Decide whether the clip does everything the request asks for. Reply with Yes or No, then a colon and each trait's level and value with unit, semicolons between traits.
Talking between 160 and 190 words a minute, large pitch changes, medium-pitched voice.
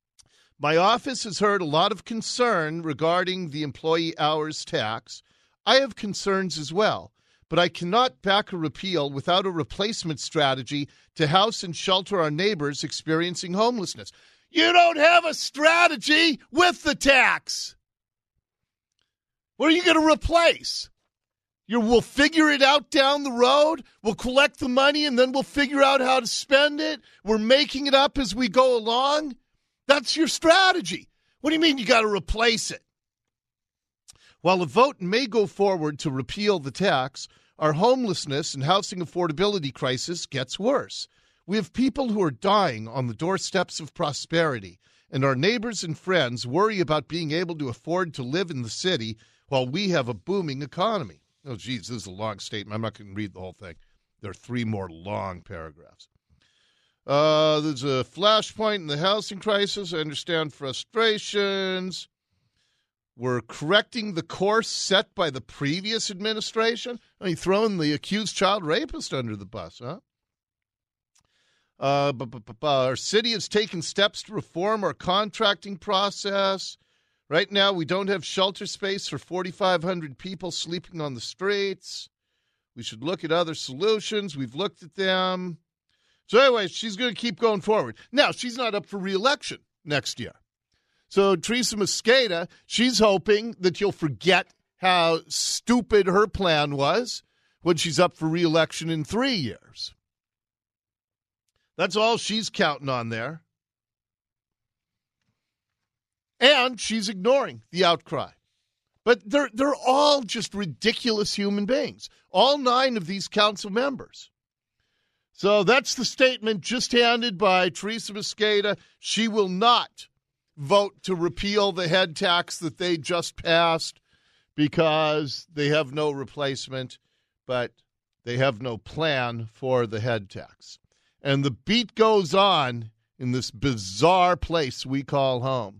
No: average, 150 wpm; wide, 7.6 semitones; medium, 180 Hz